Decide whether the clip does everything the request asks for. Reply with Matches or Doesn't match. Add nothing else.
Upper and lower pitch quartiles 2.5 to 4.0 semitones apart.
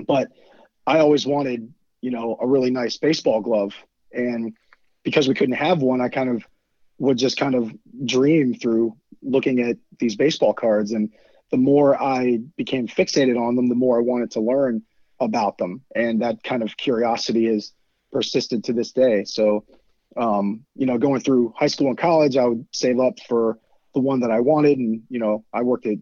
Matches